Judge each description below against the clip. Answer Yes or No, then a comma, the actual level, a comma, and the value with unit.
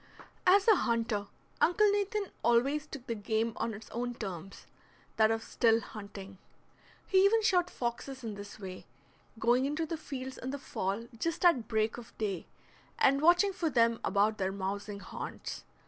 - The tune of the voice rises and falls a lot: Yes, wide, 6.3 semitones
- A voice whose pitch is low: No, high, 235 Hz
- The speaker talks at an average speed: Yes, average, 165 wpm